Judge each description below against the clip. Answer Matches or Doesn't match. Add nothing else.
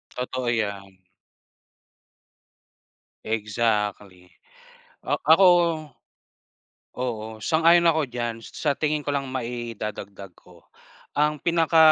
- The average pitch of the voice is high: Doesn't match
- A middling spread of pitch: Doesn't match